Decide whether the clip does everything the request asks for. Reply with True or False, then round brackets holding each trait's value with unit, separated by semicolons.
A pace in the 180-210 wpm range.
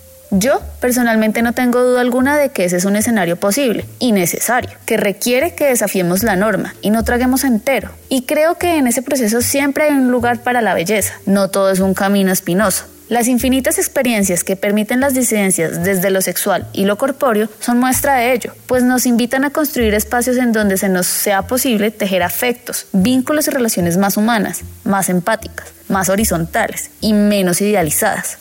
True (185 wpm)